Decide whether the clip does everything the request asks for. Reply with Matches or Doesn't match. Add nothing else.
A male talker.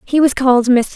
Doesn't match